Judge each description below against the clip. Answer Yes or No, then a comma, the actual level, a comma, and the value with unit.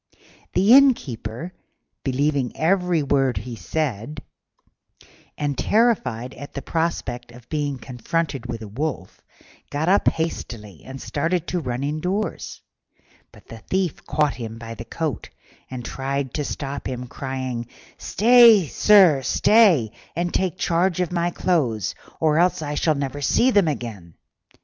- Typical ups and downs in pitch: No, wide, 5.9 semitones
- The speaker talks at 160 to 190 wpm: No, average, 140 wpm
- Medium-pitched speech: Yes, medium, 145 Hz